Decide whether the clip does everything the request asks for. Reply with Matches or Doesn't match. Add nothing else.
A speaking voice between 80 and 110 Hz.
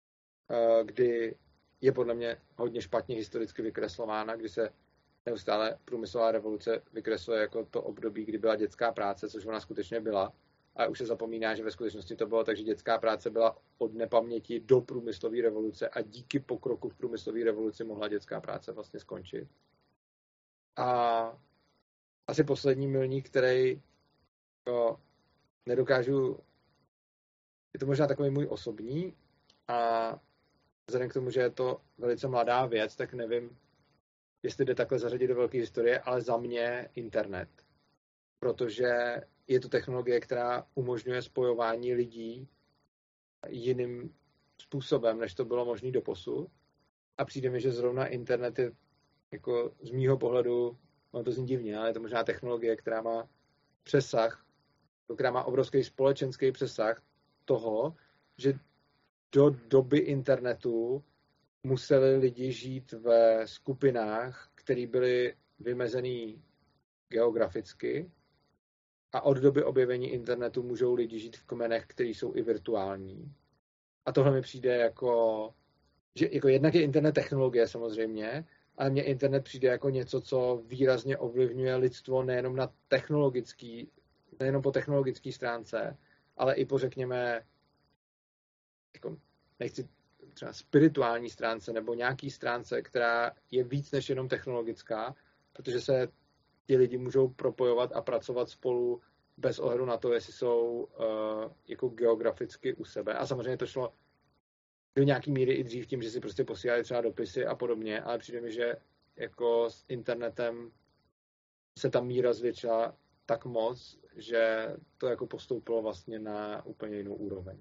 Doesn't match